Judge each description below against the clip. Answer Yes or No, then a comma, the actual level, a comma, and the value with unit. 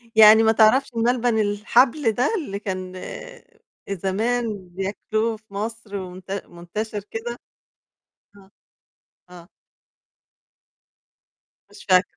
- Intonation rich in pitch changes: No, average, 2.9 semitones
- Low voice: No, high, 215 Hz